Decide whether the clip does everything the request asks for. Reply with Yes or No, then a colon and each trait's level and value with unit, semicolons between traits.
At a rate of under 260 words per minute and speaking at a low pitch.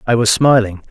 Yes: average, 200 wpm; low, 115 Hz